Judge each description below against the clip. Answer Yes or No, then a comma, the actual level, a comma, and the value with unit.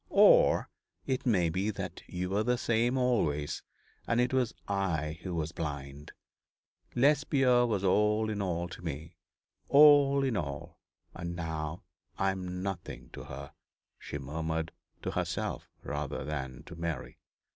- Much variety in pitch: Yes, wide, 7.1 semitones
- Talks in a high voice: No, very low, 90 Hz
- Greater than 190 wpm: No, average, 145 wpm